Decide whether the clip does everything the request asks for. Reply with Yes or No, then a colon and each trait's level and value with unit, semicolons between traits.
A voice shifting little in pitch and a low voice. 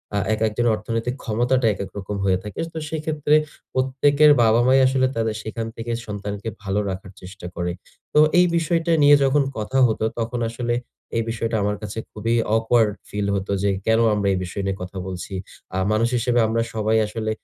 No: average, 3.1 semitones; low, 115 Hz